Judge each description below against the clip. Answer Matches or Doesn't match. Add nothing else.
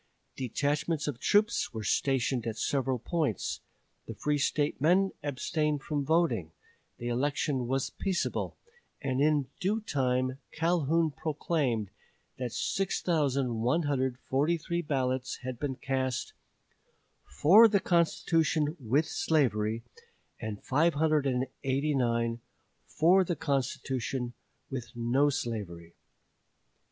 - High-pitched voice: Doesn't match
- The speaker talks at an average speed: Doesn't match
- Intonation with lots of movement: Doesn't match